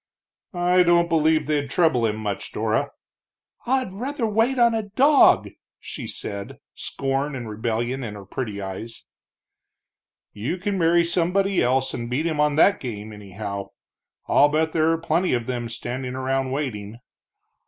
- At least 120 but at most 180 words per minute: Yes, average, 155 wpm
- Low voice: No, medium, 145 Hz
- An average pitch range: No, wide, 6.9 semitones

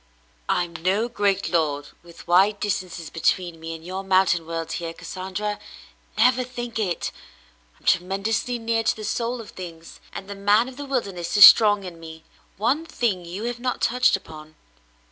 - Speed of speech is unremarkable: Yes, average, 170 wpm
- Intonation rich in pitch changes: No, average, 4.9 semitones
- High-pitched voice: Yes, high, 195 Hz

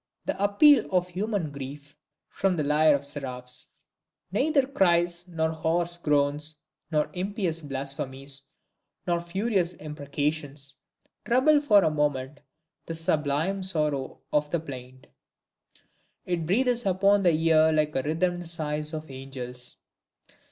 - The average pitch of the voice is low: No, medium, 160 Hz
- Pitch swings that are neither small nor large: Yes, average, 4.2 semitones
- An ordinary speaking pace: No, slow, 125 wpm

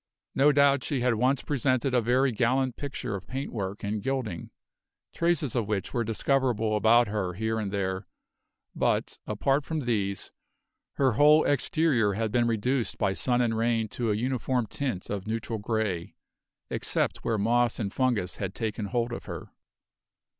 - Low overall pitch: Yes, low, 115 Hz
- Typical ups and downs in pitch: Yes, average, 3.7 semitones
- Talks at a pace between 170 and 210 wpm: No, average, 160 wpm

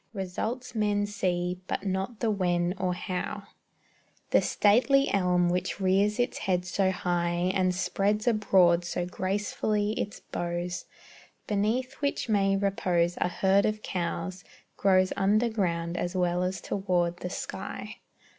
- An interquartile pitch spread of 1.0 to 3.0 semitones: Yes, narrow, 2.6 semitones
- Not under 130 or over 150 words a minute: Yes, slow, 135 wpm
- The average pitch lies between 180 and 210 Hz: Yes, high, 190 Hz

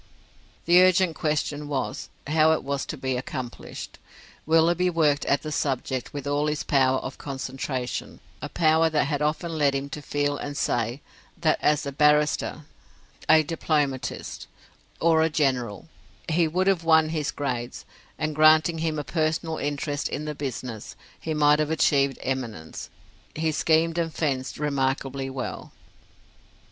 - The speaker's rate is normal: Yes, average, 150 wpm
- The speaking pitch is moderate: Yes, medium, 150 Hz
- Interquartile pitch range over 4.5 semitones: No, average, 2.8 semitones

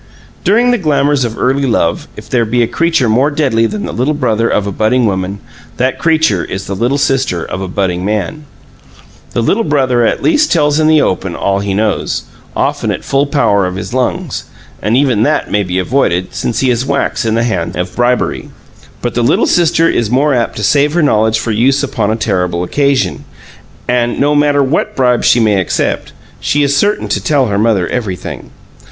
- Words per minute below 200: No, fast, 205 wpm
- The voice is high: No, low, 120 Hz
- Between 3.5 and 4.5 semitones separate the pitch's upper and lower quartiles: No, wide, 5.5 semitones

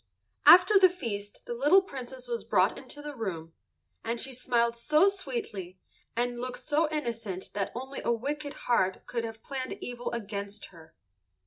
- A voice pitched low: No, high, 240 Hz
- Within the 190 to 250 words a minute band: No, average, 160 wpm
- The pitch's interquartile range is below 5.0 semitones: No, wide, 5.5 semitones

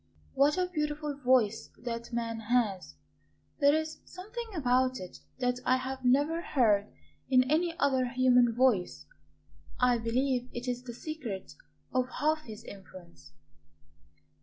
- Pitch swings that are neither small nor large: Yes, average, 3.8 semitones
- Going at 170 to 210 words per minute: No, slow, 135 wpm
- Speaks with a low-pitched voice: No, very high, 255 Hz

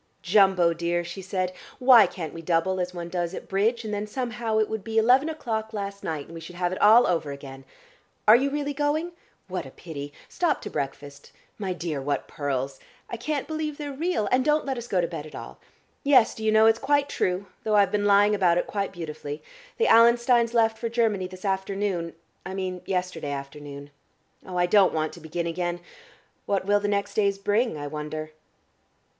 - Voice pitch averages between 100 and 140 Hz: No, high, 195 Hz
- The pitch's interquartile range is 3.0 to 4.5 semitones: No, average, 5.1 semitones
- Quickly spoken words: Yes, fast, 210 wpm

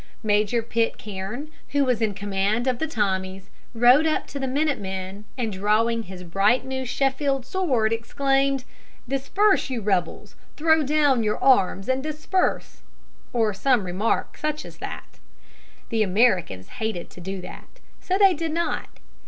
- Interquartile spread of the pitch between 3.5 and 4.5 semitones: No, wide, 5.6 semitones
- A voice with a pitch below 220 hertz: No, high, 230 Hz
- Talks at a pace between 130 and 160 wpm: Yes, average, 150 wpm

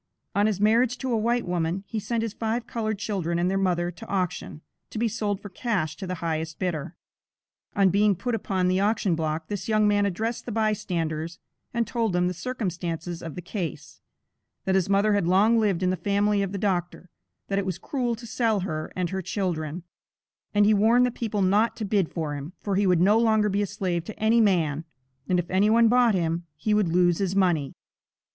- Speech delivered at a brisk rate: Yes, fast, 215 wpm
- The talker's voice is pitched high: Yes, high, 195 Hz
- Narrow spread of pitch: No, average, 3.6 semitones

